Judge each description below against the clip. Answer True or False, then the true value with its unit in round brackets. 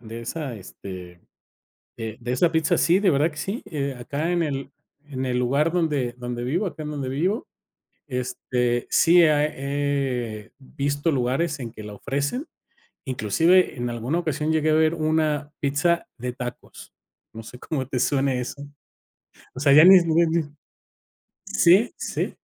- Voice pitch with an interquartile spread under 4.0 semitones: False (4.3 semitones)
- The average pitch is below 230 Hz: True (140 Hz)